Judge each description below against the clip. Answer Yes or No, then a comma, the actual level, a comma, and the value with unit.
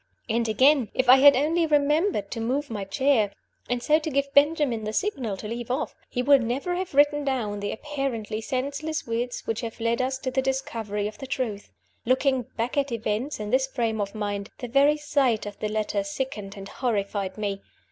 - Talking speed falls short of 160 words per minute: No, average, 200 wpm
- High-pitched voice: Yes, very high, 250 Hz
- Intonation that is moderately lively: Yes, average, 4.6 semitones